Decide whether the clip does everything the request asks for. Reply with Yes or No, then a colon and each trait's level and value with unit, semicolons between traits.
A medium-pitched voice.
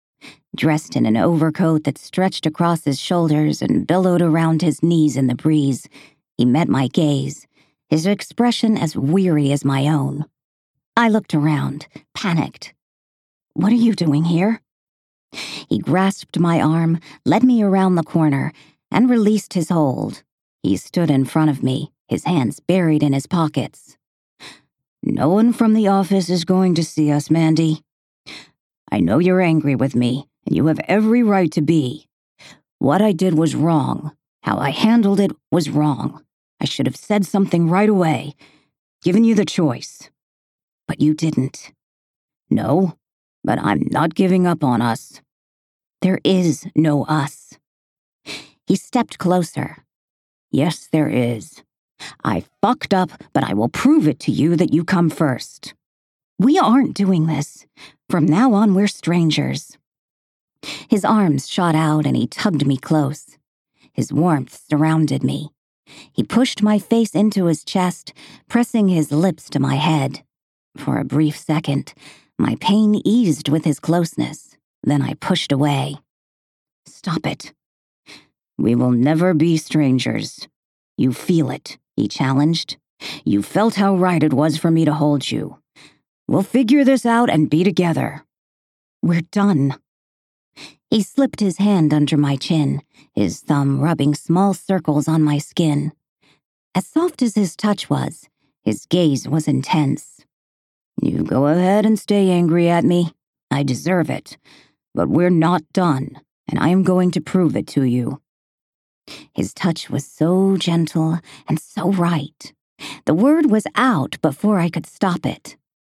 Yes: medium, 160 Hz